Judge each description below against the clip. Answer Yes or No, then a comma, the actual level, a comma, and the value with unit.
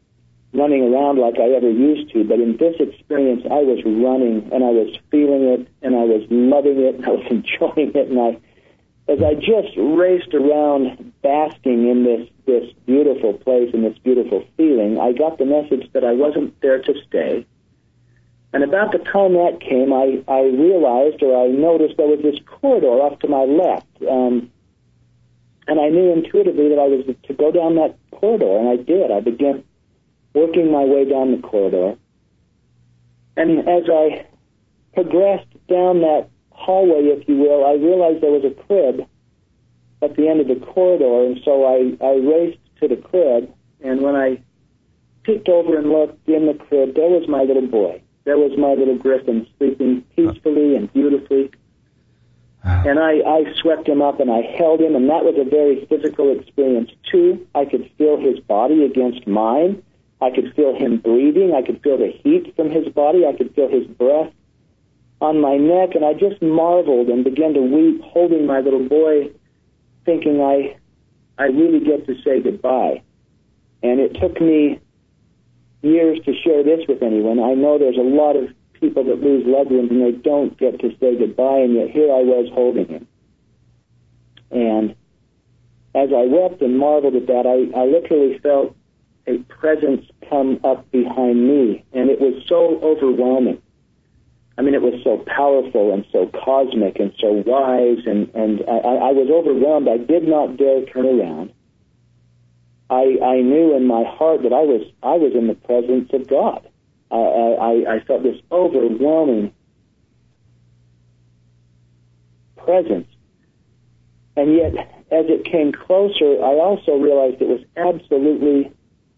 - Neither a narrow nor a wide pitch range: Yes, average, 4.1 semitones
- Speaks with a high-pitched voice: No, low, 135 Hz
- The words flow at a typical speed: Yes, average, 170 wpm